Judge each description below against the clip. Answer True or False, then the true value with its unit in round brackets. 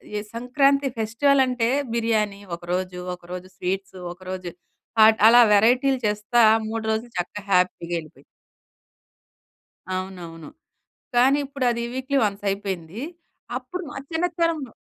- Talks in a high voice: True (220 Hz)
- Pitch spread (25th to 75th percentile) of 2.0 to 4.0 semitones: False (5.6 semitones)